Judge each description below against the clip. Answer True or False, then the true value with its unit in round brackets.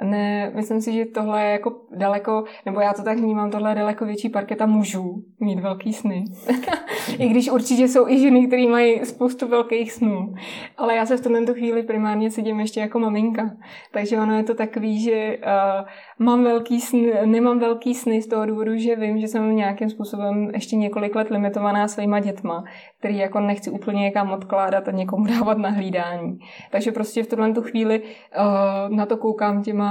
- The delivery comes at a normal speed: False (185 wpm)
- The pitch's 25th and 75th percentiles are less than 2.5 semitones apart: True (2.1 semitones)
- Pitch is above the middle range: True (215 Hz)